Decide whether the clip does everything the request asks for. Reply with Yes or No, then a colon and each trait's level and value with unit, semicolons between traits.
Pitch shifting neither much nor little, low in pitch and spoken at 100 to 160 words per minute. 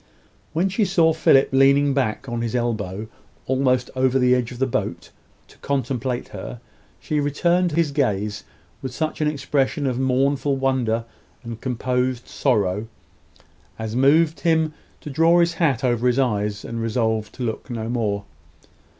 Yes: average, 3.7 semitones; low, 130 Hz; average, 155 wpm